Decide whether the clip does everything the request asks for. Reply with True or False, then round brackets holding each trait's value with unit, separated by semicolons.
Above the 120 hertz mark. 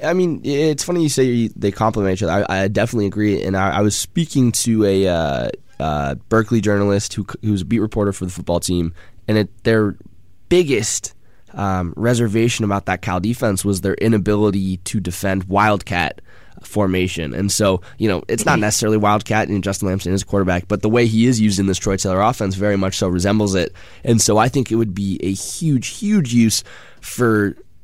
False (105 Hz)